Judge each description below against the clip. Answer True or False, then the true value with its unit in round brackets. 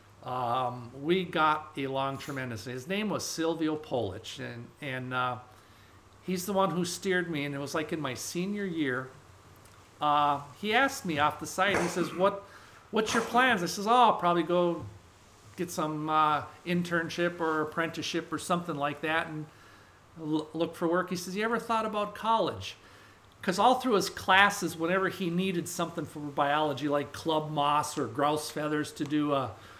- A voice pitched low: False (155 Hz)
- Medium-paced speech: True (175 wpm)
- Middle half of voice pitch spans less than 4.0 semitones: False (5.0 semitones)